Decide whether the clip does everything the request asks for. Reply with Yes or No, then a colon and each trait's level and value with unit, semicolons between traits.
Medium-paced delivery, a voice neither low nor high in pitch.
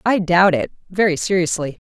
Yes: average, 160 wpm; medium, 180 Hz